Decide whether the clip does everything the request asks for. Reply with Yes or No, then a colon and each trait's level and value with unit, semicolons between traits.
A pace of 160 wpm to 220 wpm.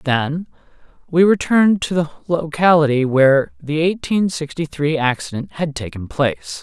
No: slow, 135 wpm